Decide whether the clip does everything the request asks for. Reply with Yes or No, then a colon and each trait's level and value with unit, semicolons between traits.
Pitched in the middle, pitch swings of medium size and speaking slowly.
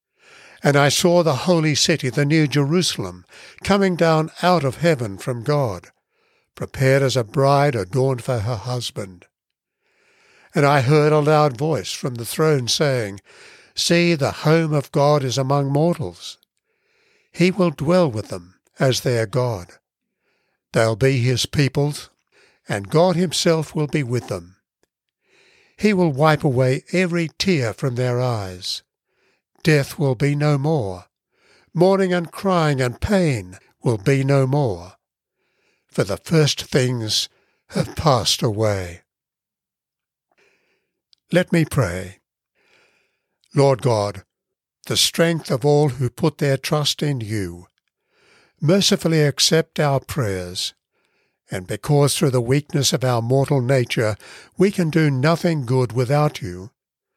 Yes: medium, 145 Hz; average, 4.8 semitones; slow, 130 wpm